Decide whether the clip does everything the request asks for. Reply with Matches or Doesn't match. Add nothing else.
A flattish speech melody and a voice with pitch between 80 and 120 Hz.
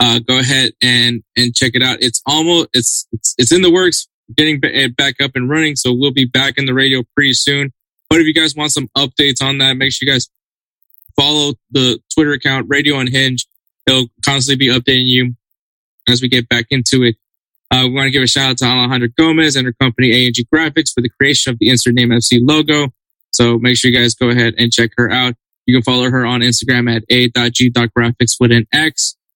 Doesn't match